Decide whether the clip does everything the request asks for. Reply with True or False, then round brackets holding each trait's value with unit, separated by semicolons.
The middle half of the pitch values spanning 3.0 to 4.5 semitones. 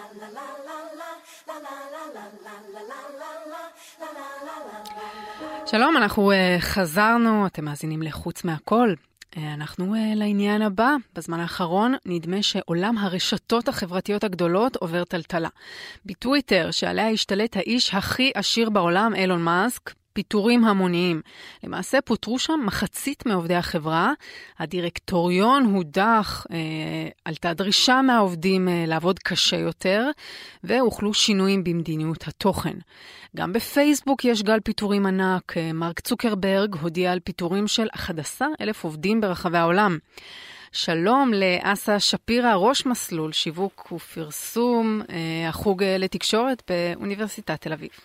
False (5.1 semitones)